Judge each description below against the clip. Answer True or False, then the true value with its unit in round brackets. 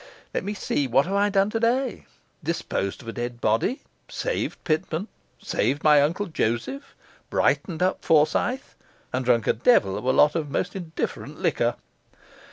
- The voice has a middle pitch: True (155 Hz)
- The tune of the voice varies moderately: False (7.9 semitones)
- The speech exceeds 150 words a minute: True (160 wpm)